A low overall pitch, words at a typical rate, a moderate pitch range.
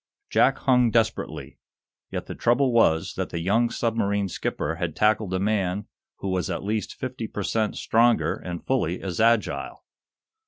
Yes: low, 105 Hz; average, 160 wpm; average, 3.9 semitones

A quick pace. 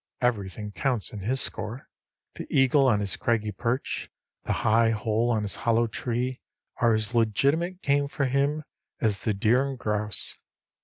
No: average, 160 wpm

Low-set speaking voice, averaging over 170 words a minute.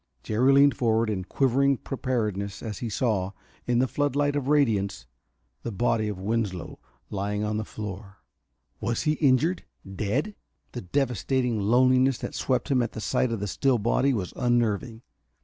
No: low, 115 Hz; average, 160 wpm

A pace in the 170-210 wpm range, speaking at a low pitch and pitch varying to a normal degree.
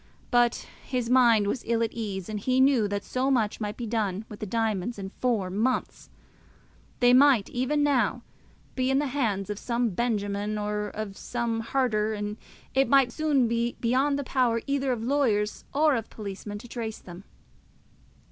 No: average, 175 wpm; high, 230 Hz; average, 3.5 semitones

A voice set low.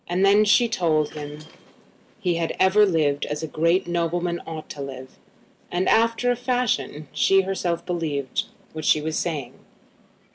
No: medium, 170 Hz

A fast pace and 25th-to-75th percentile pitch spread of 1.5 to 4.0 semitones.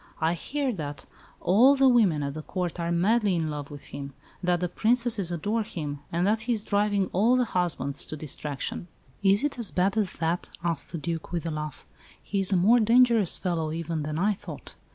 No: fast, 210 wpm; average, 5.2 semitones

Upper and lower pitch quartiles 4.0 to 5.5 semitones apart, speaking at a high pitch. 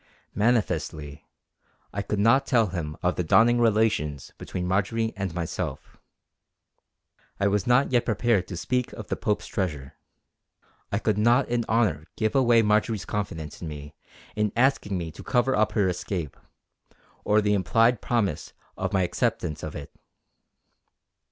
No: average, 4.7 semitones; low, 105 Hz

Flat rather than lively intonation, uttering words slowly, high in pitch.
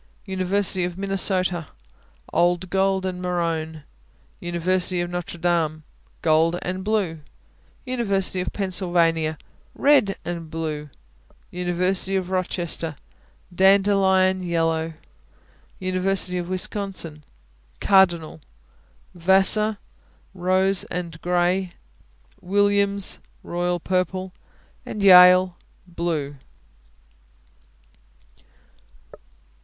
No: narrow, 1.9 semitones; slow, 75 wpm; medium, 180 Hz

